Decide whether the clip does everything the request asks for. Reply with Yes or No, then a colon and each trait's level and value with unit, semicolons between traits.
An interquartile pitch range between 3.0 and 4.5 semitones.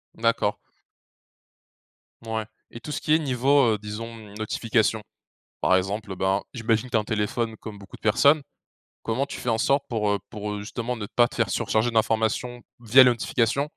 No: narrow, 2.5 semitones